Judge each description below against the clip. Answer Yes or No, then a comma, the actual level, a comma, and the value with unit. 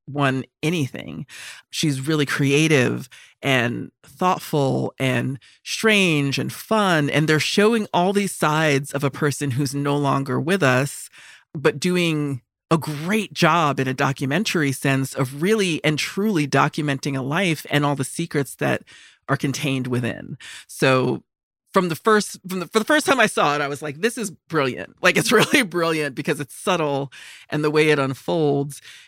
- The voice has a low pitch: No, medium, 150 Hz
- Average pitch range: Yes, average, 3.8 semitones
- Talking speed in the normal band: Yes, average, 165 wpm